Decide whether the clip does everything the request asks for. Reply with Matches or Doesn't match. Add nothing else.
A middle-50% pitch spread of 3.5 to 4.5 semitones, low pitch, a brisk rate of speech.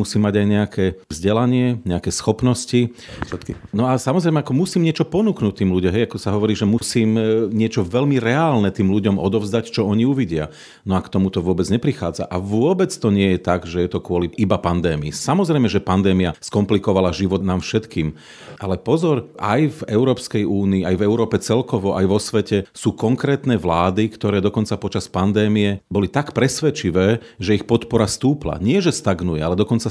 Matches